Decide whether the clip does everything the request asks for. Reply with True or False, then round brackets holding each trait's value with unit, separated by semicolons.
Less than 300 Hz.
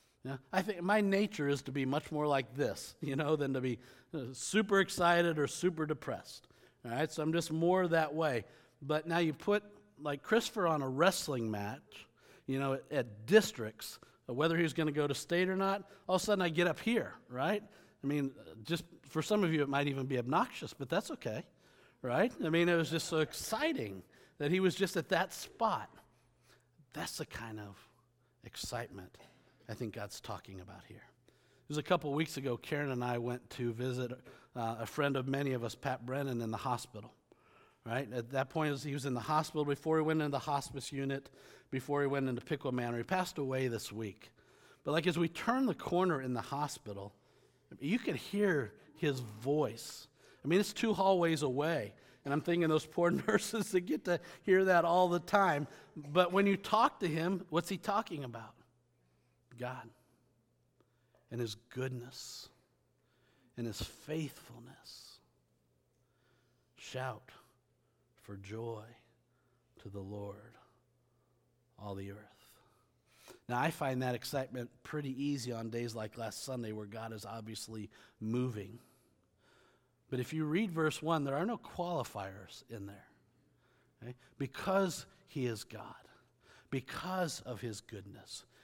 True (140 Hz)